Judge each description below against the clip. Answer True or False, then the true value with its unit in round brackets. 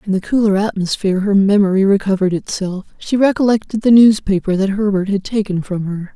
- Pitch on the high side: True (200 Hz)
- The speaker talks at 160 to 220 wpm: True (175 wpm)